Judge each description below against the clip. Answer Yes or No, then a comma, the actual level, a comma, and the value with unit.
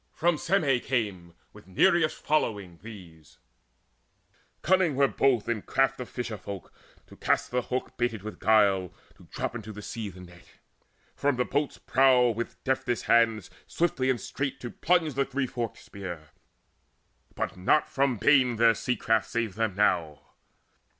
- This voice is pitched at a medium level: No, low, 115 Hz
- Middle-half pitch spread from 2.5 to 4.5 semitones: No, average, 4.9 semitones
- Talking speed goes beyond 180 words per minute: No, average, 155 wpm